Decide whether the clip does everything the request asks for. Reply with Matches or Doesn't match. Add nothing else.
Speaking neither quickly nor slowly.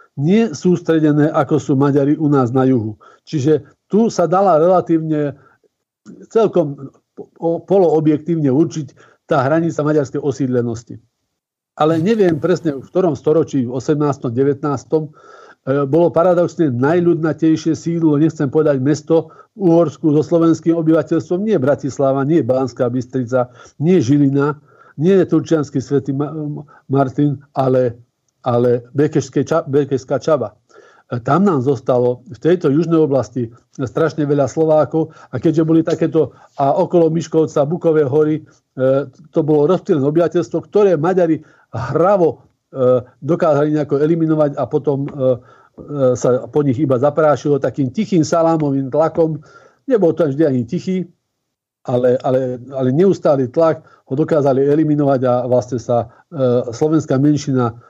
Matches